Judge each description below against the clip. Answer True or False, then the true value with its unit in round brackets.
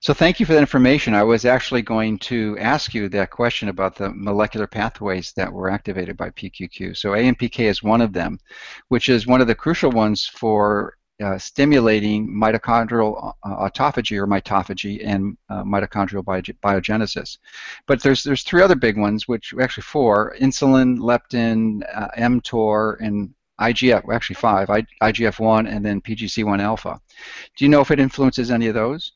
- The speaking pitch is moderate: False (110 Hz)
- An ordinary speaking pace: True (165 wpm)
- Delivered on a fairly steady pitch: False (3.3 semitones)